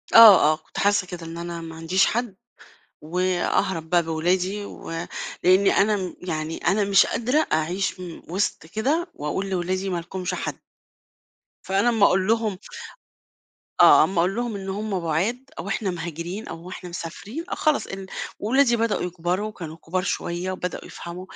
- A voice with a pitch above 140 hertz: Yes, medium, 185 Hz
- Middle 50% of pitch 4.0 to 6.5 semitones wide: No, average, 3.1 semitones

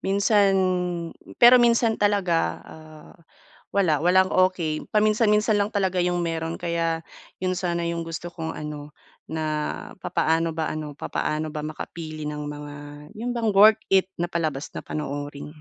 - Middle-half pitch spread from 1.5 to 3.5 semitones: No, average, 4.2 semitones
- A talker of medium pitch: Yes, medium, 170 Hz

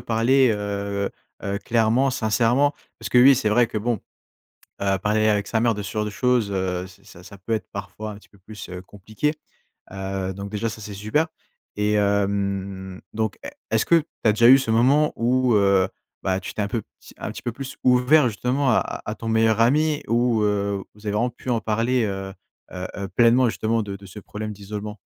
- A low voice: Yes, low, 105 Hz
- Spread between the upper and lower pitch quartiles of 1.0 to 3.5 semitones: Yes, average, 3.1 semitones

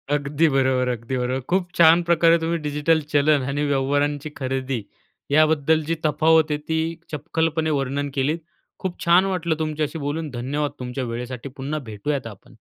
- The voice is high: No, medium, 145 Hz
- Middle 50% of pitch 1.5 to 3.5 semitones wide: Yes, average, 3.1 semitones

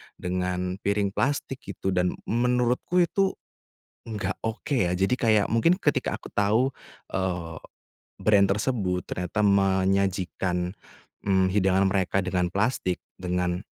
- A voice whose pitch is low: Yes, very low, 95 Hz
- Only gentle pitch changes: No, average, 3.1 semitones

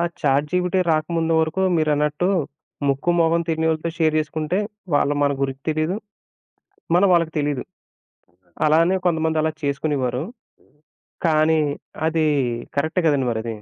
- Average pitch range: No, narrow, 2.1 semitones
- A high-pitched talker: No, medium, 155 Hz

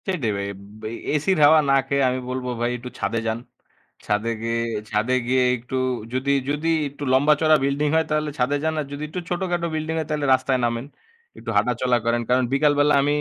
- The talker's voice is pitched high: No, medium, 140 Hz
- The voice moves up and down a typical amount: Yes, average, 3.6 semitones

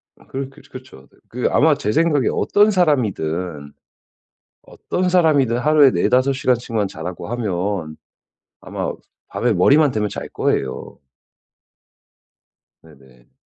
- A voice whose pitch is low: Yes, low, 120 Hz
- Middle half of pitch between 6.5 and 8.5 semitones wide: Yes, wide, 8.0 semitones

